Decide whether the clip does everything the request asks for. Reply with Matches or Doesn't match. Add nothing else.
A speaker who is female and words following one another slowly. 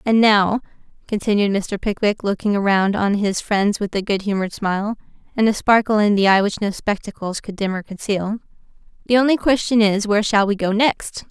Doesn't match